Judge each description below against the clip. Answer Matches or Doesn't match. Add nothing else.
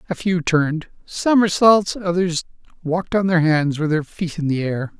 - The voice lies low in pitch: Doesn't match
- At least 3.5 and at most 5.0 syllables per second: Matches